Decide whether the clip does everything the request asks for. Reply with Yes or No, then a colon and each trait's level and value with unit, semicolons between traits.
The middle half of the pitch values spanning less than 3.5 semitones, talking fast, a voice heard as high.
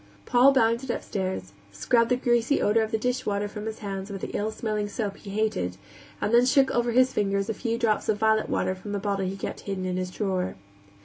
Yes: average, 3.1 semitones; fast, 225 wpm; high, 215 Hz